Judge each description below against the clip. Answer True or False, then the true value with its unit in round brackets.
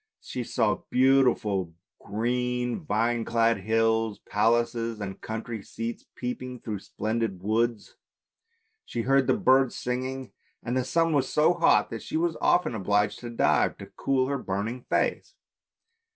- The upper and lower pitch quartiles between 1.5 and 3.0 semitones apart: True (2.7 semitones)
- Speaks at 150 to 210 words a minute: False (140 wpm)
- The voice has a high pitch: False (120 Hz)